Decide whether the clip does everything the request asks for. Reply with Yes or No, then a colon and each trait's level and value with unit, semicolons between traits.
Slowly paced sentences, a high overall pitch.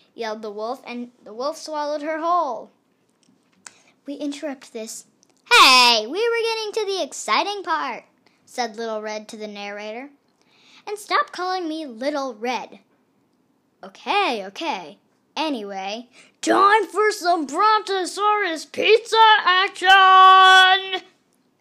Yes: slow, 115 wpm; very high, 315 Hz